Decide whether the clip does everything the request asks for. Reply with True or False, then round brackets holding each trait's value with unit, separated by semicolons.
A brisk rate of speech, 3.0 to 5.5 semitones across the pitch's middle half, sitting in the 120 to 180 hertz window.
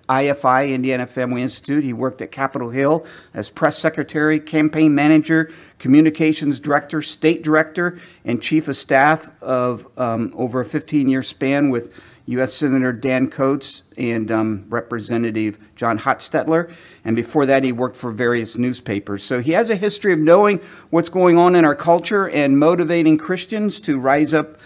False (160 wpm; 4.0 semitones; 140 Hz)